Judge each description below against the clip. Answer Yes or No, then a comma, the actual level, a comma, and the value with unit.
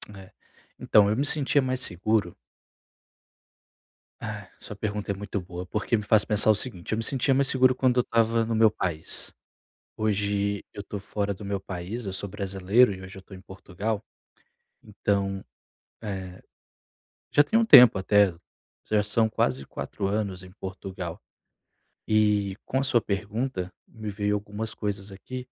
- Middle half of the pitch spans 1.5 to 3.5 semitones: Yes, average, 2.7 semitones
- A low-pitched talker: Yes, low, 105 Hz